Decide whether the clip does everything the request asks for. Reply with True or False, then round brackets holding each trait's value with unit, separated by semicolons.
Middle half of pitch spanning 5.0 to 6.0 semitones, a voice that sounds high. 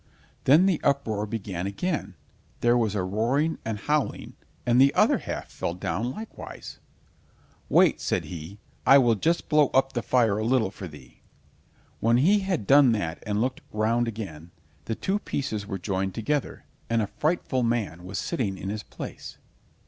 False (5.4 semitones; 115 Hz)